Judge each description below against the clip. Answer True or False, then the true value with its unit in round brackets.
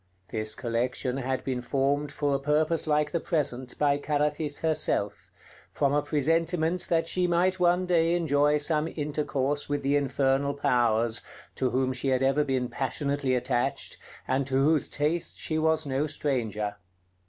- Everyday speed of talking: True (155 wpm)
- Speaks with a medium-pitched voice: True (145 Hz)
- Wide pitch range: False (2.9 semitones)